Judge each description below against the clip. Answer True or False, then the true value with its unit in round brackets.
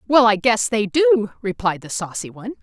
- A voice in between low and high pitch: False (215 Hz)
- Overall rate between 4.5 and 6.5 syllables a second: True (5.3 syllables/s)